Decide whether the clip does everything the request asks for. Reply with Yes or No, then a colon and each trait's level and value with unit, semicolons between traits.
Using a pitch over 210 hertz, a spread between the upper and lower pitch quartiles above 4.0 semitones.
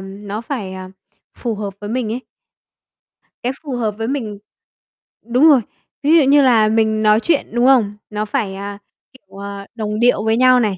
No: high, 220 Hz; average, 3.5 semitones